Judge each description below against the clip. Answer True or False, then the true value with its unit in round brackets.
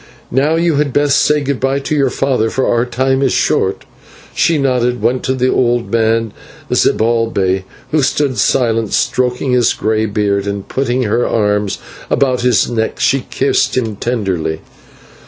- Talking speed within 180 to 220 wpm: False (160 wpm)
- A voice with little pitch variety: False (3.3 semitones)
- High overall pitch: False (125 Hz)